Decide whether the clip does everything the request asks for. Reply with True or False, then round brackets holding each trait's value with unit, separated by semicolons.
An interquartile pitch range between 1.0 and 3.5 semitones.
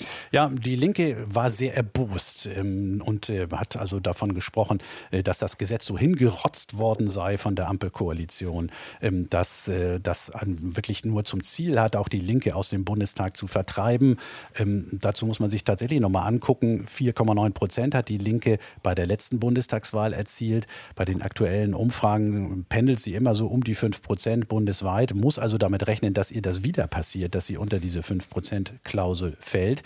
True (3.1 semitones)